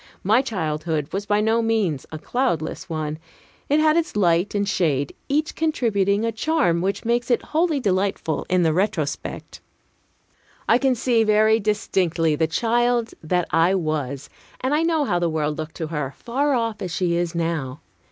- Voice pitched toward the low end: No, high, 195 Hz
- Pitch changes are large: Yes, wide, 6.5 semitones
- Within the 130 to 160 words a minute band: No, average, 170 wpm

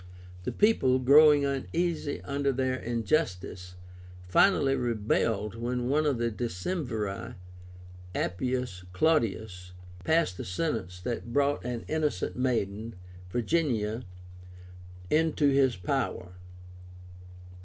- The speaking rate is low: Yes, slow, 95 wpm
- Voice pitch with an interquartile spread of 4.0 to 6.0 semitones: Yes, average, 5.1 semitones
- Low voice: Yes, low, 125 Hz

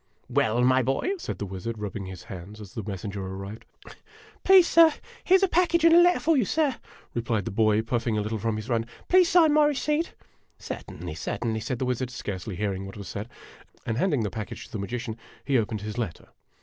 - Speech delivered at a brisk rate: Yes, fast, 225 wpm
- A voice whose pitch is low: Yes, low, 115 Hz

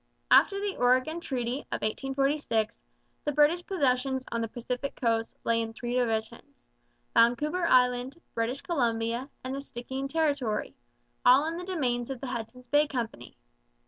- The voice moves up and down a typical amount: Yes, average, 3.7 semitones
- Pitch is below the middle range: No, very high, 255 Hz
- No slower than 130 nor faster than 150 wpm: Yes, average, 145 wpm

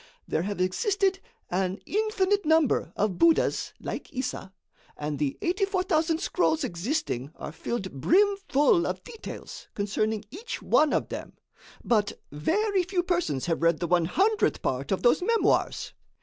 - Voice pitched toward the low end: No, very high, 290 Hz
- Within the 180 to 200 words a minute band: No, average, 145 wpm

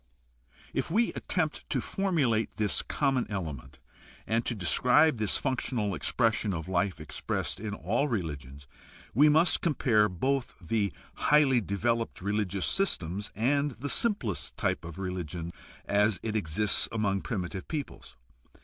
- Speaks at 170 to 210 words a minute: No, slow, 135 wpm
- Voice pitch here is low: Yes, low, 110 Hz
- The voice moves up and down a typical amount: No, wide, 6.3 semitones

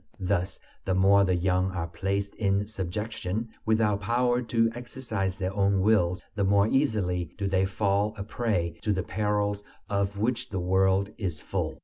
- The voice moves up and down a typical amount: No, narrow, 2.3 semitones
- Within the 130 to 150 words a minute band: No, average, 165 wpm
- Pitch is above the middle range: No, low, 100 Hz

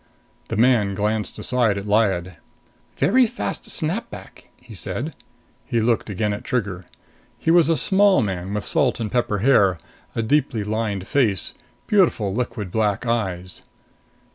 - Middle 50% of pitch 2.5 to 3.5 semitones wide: No, average, 4.0 semitones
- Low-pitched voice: Yes, low, 110 Hz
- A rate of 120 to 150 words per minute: Yes, average, 145 wpm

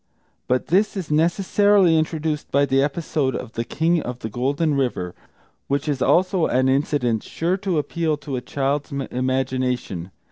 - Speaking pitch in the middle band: Yes, medium, 145 Hz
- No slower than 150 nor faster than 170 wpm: Yes, average, 155 wpm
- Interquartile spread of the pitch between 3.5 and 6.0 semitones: Yes, average, 4.2 semitones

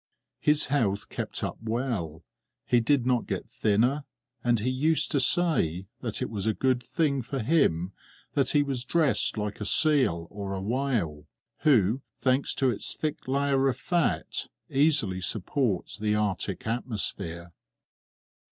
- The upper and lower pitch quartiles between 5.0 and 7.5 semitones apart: Yes, wide, 5.6 semitones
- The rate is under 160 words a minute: Yes, average, 150 wpm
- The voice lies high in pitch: No, low, 120 Hz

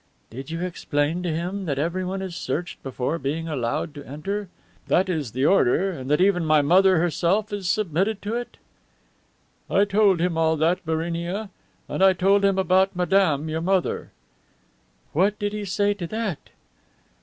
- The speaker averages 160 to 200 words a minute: Yes, average, 170 wpm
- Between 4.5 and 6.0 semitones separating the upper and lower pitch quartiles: No, average, 3.6 semitones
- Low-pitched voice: No, medium, 180 Hz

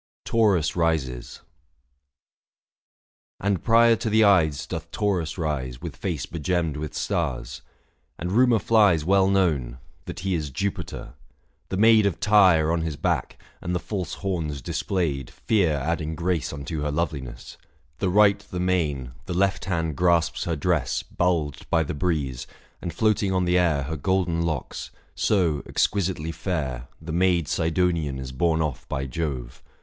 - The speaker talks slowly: No, average, 160 wpm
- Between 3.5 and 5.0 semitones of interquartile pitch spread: Yes, average, 4.1 semitones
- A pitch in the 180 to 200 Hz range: No, very low, 85 Hz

